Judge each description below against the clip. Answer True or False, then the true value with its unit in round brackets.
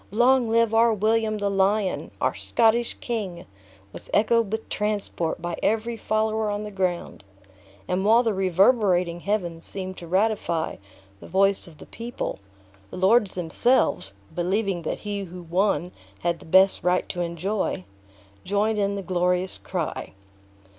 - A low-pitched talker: False (195 Hz)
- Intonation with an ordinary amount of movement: True (3.5 semitones)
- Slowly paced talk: False (145 wpm)